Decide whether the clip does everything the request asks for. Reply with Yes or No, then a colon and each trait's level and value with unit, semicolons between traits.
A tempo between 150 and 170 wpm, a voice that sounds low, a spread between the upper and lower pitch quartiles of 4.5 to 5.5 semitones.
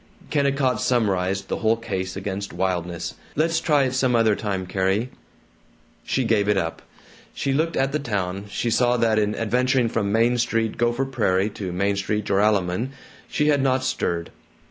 Yes: average, 165 wpm; low, 110 Hz; average, 4.9 semitones